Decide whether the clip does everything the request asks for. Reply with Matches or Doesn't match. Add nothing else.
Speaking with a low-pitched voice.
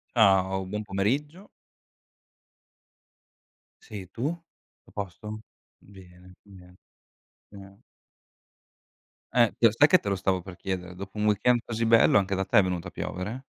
Matches